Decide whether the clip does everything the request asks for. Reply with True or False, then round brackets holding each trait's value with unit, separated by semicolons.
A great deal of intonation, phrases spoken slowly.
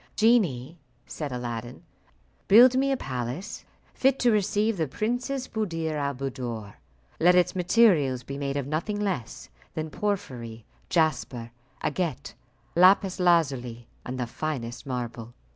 True (8.3 semitones; 125 wpm)